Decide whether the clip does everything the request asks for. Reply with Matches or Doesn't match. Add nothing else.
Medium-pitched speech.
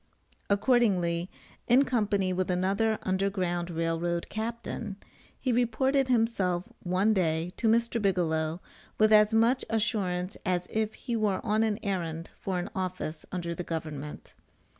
Doesn't match